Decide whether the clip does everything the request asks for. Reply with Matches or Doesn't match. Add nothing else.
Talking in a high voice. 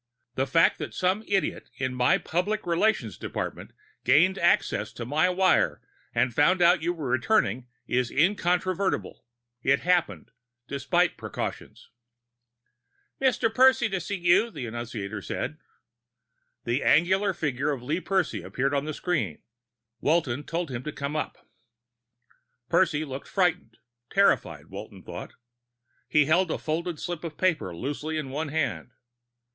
Doesn't match